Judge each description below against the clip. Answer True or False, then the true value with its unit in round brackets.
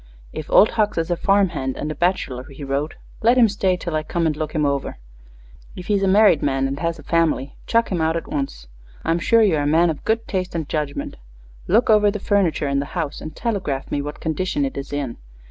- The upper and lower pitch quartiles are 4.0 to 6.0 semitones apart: True (5.3 semitones)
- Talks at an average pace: False (240 wpm)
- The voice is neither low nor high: True (165 Hz)